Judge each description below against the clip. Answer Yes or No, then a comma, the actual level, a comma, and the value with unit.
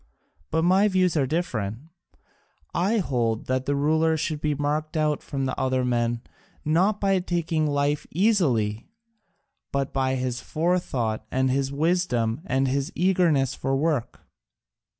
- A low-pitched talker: No, medium, 145 Hz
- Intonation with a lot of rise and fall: No, average, 4.5 semitones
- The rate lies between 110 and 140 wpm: Yes, slow, 135 wpm